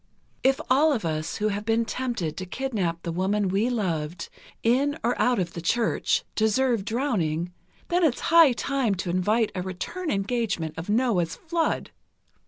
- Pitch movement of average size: No, wide, 6.1 semitones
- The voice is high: Yes, high, 215 Hz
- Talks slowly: No, average, 165 wpm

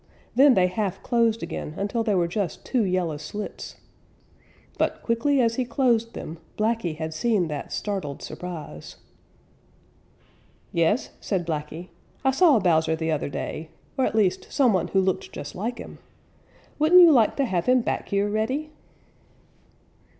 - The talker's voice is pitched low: No, high, 205 Hz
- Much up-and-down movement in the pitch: Yes, wide, 5.9 semitones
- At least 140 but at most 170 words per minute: Yes, average, 155 wpm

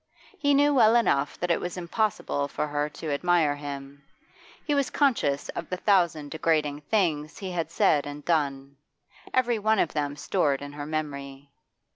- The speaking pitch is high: No, medium, 155 Hz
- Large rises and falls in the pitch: No, average, 4.9 semitones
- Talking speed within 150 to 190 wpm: Yes, average, 170 wpm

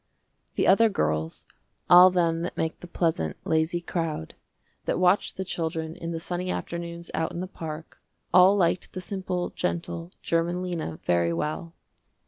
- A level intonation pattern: Yes, narrow, 1.9 semitones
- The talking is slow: No, average, 155 wpm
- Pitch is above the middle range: No, medium, 170 Hz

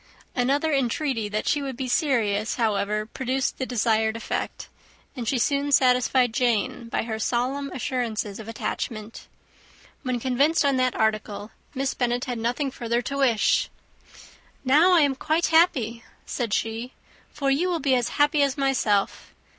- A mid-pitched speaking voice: No, very high, 250 Hz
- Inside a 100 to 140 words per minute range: No, average, 155 wpm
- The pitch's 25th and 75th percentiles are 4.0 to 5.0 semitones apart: No, average, 3.5 semitones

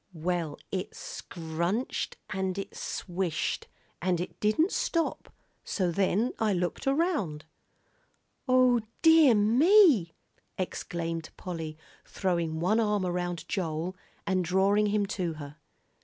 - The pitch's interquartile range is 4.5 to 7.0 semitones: No, average, 4.1 semitones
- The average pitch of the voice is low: No, medium, 185 Hz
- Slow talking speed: Yes, slow, 110 wpm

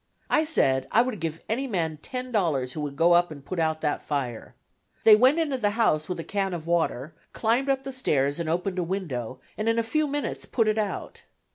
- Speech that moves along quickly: Yes, fast, 225 wpm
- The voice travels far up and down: Yes, wide, 6.9 semitones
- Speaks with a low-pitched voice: No, medium, 180 Hz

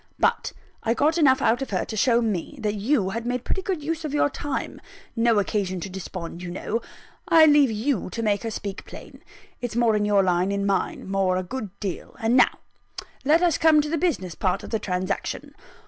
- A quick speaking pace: Yes, fast, 215 wpm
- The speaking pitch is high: Yes, high, 225 Hz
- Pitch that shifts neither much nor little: No, wide, 6.6 semitones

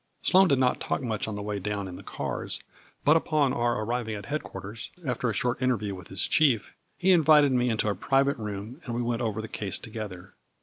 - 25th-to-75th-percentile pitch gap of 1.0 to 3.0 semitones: No, average, 4.5 semitones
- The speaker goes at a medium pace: No, fast, 225 wpm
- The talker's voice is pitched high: No, low, 115 Hz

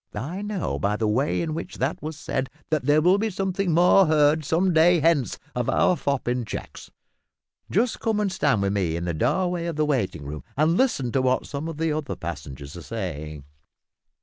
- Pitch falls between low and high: Yes, medium, 150 Hz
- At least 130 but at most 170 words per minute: No, fast, 205 wpm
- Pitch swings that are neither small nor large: No, wide, 7.6 semitones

